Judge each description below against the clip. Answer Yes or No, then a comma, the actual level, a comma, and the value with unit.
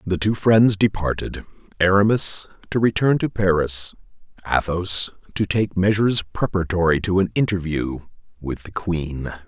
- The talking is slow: Yes, slow, 120 wpm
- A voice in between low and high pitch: No, very low, 95 Hz